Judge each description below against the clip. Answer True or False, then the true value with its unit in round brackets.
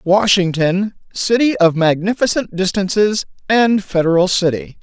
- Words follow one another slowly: True (100 wpm)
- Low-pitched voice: False (195 Hz)